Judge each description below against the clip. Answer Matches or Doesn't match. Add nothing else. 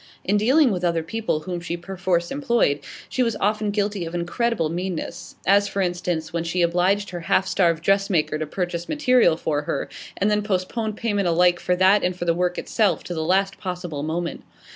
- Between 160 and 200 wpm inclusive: Matches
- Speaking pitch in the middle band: Matches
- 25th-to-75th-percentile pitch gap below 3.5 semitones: Matches